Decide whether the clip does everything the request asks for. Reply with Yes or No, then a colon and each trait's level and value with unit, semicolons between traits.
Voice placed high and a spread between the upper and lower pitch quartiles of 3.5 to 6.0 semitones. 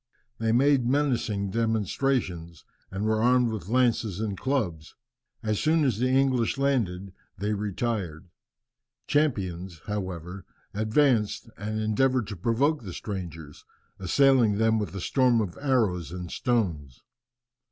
No: low, 110 Hz; average, 5.1 semitones